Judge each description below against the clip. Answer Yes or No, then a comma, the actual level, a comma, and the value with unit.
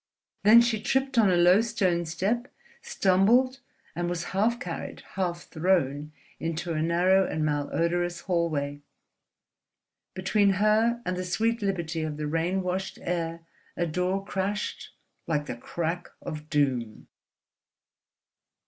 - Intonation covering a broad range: No, average, 3.6 semitones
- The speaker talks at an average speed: No, slow, 130 wpm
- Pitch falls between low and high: Yes, medium, 180 Hz